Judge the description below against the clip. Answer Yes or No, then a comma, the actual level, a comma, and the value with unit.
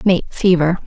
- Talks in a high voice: No, medium, 175 Hz